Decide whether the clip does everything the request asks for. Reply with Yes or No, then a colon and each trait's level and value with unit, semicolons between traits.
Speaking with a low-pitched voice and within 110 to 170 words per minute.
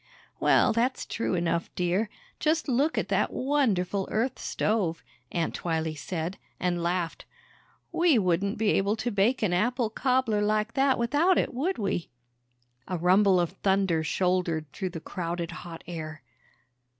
No: high, 195 Hz; average, 150 wpm